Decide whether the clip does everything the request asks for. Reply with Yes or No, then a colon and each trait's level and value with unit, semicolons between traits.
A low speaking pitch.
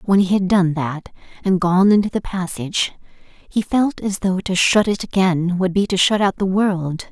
No: high, 190 Hz